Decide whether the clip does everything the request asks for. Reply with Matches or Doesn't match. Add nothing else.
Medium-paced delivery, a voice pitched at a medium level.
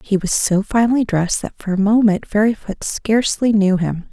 Doesn't match